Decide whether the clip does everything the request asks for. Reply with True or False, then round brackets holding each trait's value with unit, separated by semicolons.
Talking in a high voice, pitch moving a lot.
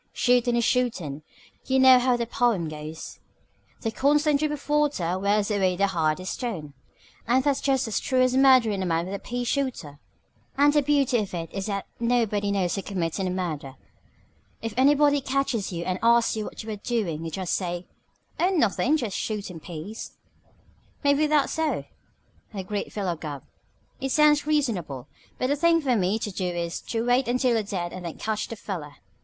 True (220 Hz; 6.3 semitones)